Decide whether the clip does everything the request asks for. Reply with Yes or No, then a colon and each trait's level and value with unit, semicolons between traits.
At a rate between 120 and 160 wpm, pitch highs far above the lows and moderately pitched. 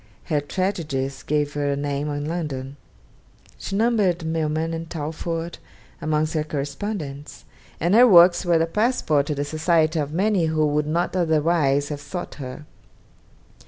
No: average, 150 wpm; average, 3.0 semitones; medium, 155 Hz